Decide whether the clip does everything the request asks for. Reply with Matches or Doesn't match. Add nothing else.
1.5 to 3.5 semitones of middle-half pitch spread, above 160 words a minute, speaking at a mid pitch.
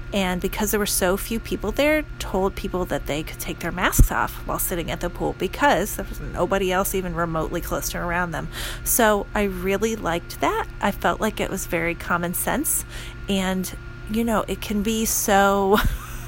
Matches